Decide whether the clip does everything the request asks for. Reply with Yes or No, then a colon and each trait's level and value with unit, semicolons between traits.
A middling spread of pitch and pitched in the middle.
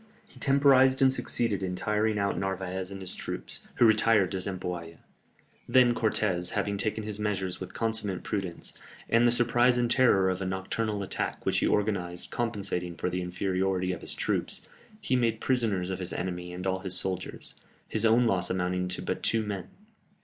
No: average, 3.7 semitones; low, 100 Hz